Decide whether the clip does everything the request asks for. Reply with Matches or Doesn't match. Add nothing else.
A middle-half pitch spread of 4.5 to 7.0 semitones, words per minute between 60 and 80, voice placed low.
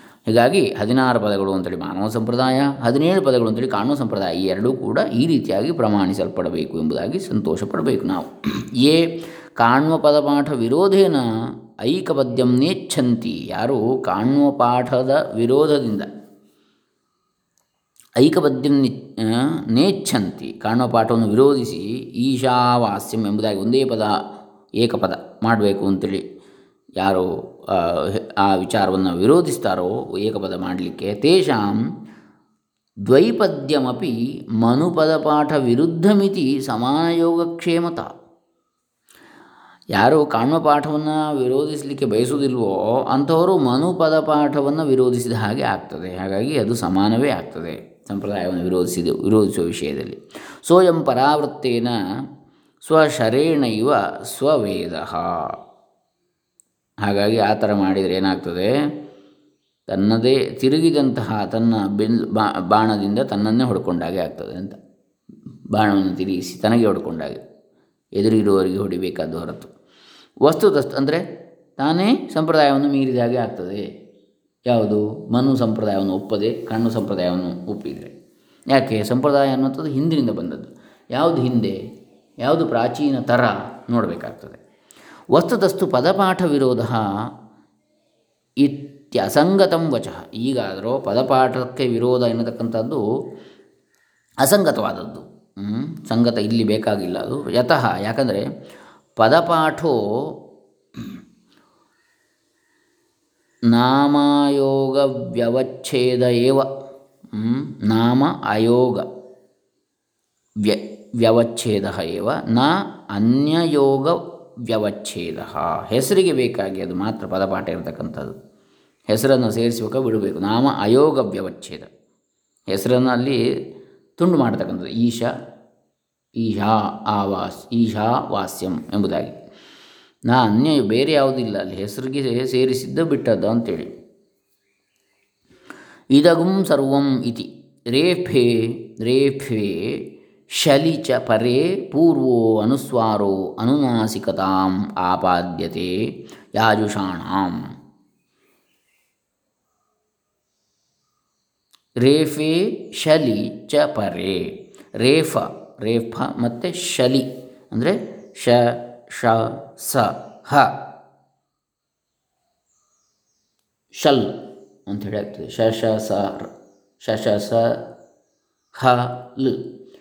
Matches